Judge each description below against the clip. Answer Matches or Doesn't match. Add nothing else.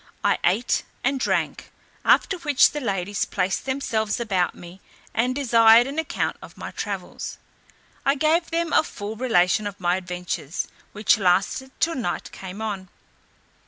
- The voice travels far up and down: Matches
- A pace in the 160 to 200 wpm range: Doesn't match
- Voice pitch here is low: Doesn't match